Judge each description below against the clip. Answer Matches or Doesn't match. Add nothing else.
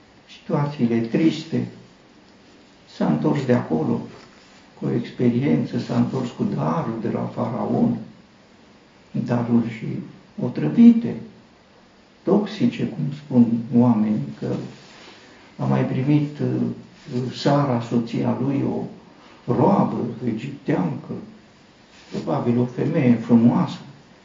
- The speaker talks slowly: Matches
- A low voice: Matches